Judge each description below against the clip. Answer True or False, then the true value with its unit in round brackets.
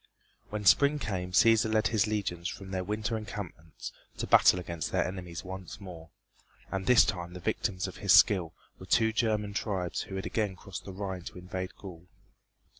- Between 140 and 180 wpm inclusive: False (190 wpm)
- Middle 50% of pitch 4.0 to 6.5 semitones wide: False (2.9 semitones)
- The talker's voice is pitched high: False (95 Hz)